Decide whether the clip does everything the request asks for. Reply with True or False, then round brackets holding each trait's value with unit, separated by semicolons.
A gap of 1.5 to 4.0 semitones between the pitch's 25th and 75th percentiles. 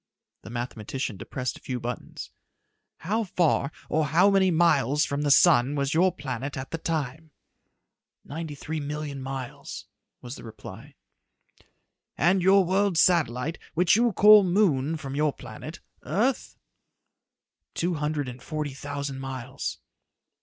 False (4.5 semitones)